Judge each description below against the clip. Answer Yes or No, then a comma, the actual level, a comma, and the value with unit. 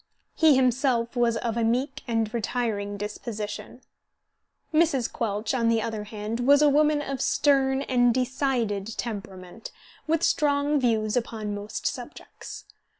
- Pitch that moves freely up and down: No, average, 3.9 semitones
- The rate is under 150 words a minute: Yes, slow, 135 wpm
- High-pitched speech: Yes, high, 235 Hz